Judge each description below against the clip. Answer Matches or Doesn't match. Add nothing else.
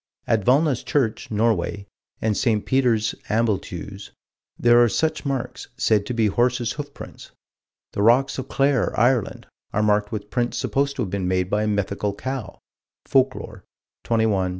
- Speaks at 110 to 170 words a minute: Matches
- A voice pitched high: Doesn't match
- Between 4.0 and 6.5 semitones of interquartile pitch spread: Doesn't match